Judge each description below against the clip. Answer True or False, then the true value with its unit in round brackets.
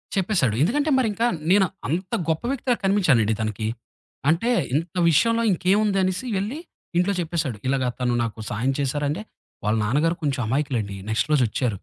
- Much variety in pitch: True (7.7 semitones)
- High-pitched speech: False (160 Hz)